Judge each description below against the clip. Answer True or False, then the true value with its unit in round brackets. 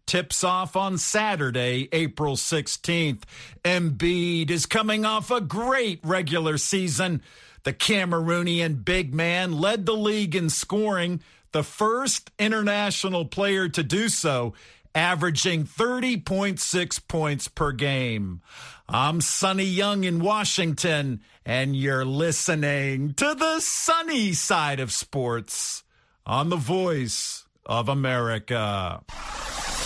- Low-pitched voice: False (170 Hz)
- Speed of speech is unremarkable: False (110 wpm)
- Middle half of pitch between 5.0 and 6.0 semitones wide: True (5.6 semitones)